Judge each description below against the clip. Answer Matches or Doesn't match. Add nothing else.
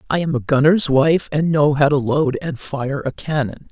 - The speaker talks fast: Matches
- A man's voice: Doesn't match